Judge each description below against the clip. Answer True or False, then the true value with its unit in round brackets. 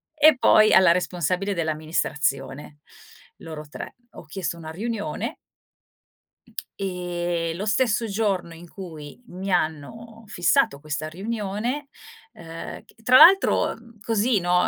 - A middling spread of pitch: True (5.0 semitones)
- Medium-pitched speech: True (180 Hz)